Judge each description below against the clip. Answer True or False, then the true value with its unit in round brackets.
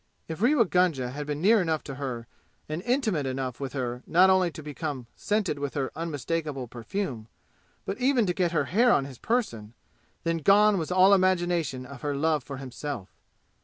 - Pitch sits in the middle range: True (155 Hz)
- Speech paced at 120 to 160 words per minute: False (185 wpm)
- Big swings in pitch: True (5.7 semitones)